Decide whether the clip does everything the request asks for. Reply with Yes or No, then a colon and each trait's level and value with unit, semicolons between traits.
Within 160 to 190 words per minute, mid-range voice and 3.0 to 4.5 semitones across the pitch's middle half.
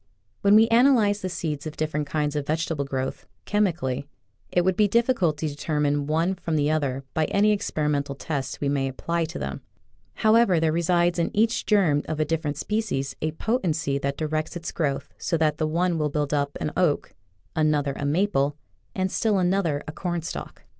Yes: average, 185 wpm; medium, 155 Hz; average, 3.9 semitones